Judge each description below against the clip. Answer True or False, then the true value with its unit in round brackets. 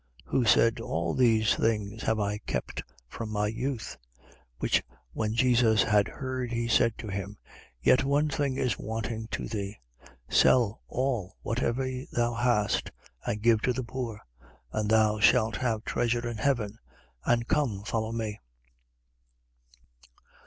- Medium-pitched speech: False (115 Hz)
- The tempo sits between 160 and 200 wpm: False (145 wpm)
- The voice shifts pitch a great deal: False (2.4 semitones)